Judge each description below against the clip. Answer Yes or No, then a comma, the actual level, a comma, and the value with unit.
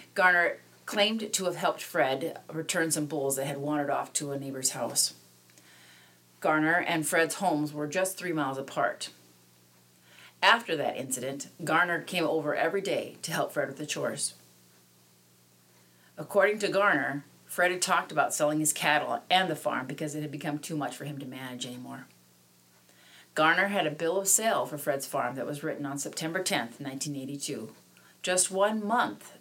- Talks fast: No, average, 170 wpm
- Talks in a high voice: No, medium, 140 Hz